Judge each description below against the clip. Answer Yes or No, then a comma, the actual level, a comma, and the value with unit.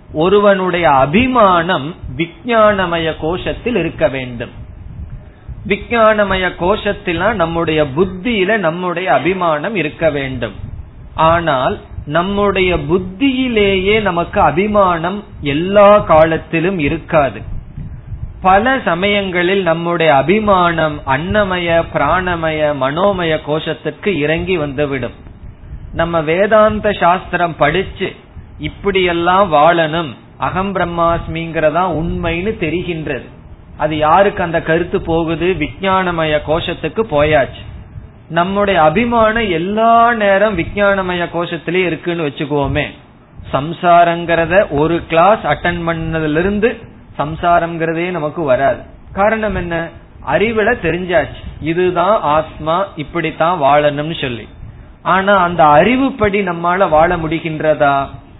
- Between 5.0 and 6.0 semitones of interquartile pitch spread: No, average, 3.9 semitones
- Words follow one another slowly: No, average, 85 wpm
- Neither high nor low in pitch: Yes, medium, 170 Hz